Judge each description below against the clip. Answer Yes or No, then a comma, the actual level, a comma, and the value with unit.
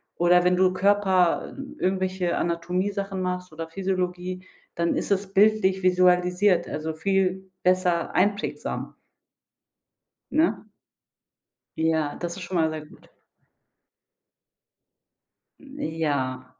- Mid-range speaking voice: Yes, medium, 180 Hz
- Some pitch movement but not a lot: No, narrow, 2.1 semitones